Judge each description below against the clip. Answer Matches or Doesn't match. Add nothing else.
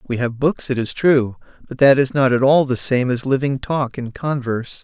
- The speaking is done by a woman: Doesn't match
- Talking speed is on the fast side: Matches